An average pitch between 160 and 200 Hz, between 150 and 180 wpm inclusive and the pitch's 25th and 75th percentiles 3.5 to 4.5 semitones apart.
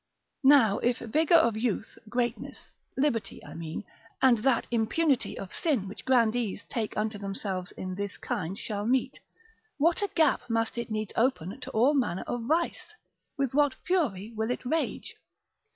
No: high, 235 Hz; average, 160 wpm; average, 4.1 semitones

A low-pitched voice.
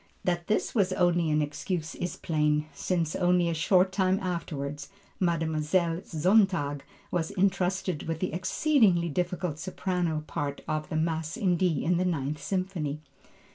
No: medium, 170 Hz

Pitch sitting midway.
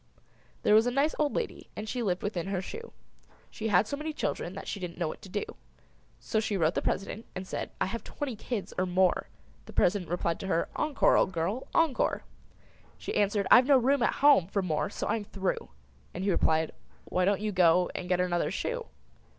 No: high, 200 Hz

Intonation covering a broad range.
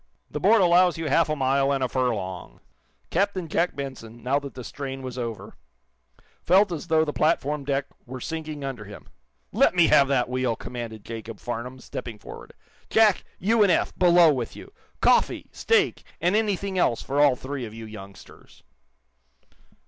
Yes: wide, 5.8 semitones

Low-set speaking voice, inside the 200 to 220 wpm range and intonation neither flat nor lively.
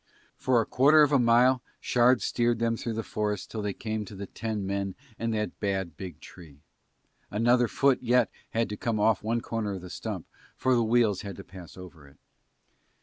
Yes: low, 110 Hz; fast, 205 wpm; average, 3.3 semitones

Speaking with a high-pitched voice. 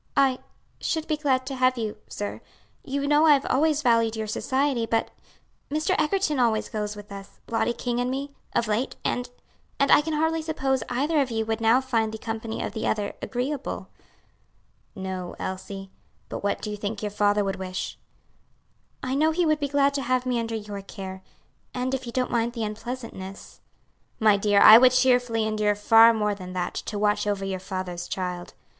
Yes: high, 230 Hz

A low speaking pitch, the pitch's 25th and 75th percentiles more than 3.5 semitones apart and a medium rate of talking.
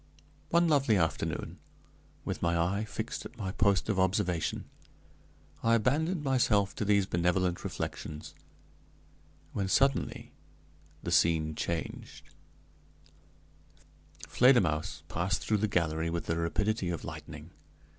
No: very low, 95 Hz; average, 4.7 semitones; slow, 115 wpm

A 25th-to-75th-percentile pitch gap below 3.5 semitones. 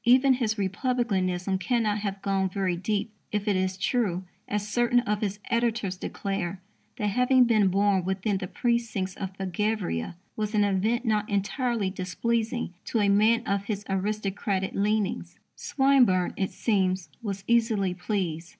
Yes: average, 3.1 semitones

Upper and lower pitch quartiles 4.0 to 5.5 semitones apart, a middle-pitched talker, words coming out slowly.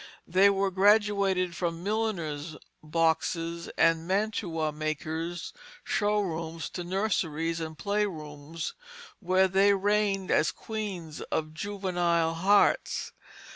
No: average, 3.6 semitones; medium, 175 Hz; slow, 105 wpm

